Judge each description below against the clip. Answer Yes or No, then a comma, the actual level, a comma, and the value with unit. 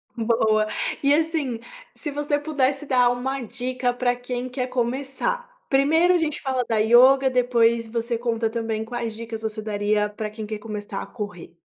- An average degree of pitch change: Yes, average, 3.3 semitones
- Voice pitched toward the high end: Yes, high, 245 Hz